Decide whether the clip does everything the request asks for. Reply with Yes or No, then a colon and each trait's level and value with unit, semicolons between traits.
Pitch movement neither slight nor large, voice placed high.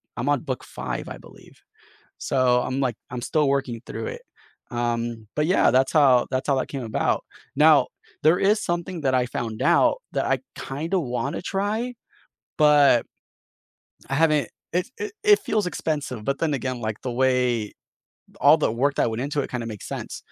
No: average, 4.1 semitones; low, 135 Hz